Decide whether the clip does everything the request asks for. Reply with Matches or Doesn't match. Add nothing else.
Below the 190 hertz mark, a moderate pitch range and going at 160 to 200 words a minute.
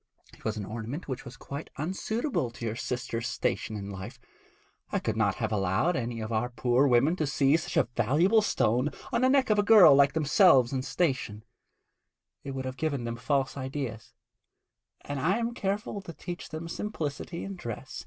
Doesn't match